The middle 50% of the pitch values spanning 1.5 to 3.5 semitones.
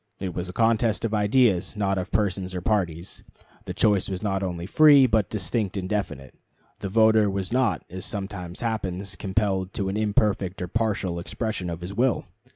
Yes: average, 2.9 semitones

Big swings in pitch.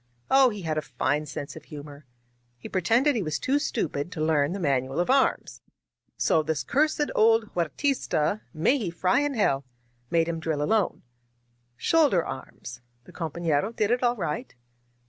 Yes: wide, 7.7 semitones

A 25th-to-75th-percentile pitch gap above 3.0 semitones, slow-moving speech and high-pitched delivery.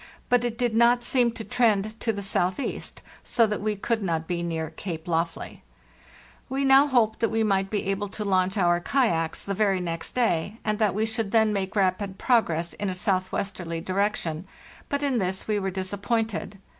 No: average, 3.5 semitones; average, 195 wpm; high, 200 Hz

